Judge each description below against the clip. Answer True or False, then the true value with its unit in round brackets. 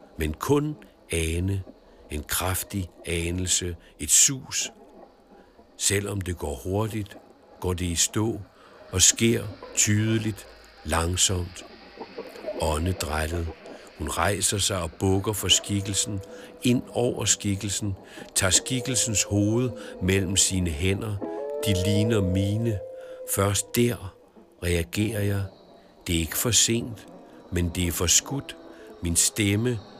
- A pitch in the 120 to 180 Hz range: False (100 Hz)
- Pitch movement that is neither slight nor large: True (3.7 semitones)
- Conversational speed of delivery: False (110 wpm)